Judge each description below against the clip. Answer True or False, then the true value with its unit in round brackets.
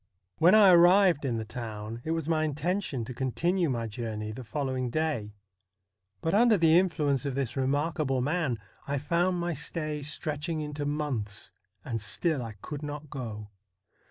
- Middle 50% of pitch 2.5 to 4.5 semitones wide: False (5.1 semitones)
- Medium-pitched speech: True (145 Hz)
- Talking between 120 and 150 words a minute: False (165 wpm)